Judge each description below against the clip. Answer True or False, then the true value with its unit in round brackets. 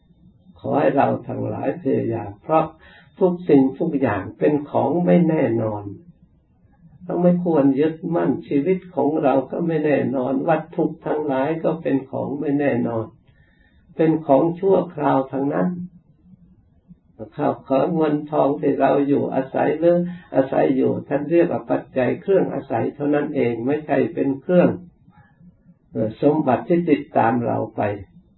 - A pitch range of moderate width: True (4.3 semitones)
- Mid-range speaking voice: True (150 Hz)